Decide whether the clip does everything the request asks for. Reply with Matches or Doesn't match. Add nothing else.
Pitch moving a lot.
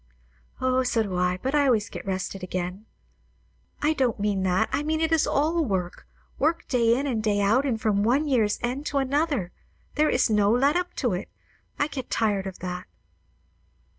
Matches